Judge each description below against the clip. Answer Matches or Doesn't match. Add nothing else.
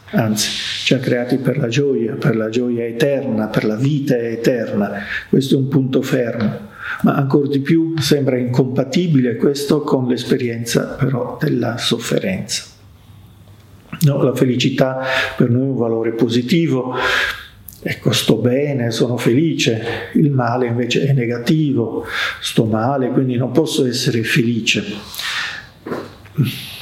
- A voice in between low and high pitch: Doesn't match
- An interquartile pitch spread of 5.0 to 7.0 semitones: Doesn't match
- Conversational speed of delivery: Matches